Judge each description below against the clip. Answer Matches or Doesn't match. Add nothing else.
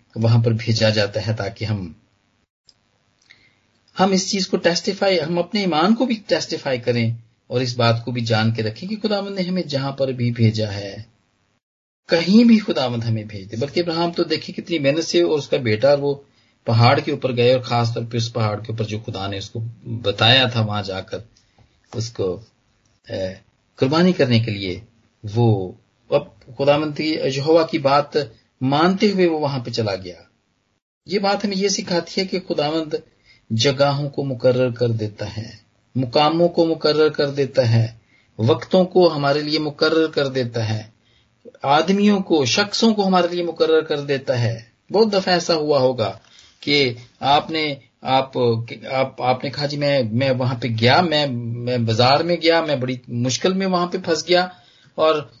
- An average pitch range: Doesn't match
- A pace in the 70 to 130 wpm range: Doesn't match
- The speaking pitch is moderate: Doesn't match